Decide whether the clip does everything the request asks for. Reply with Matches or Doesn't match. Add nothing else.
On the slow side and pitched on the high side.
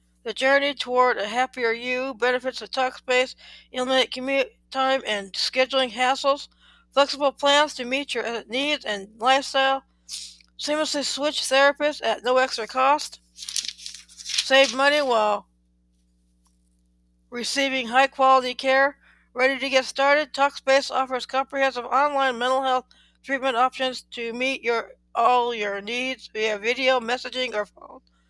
Matches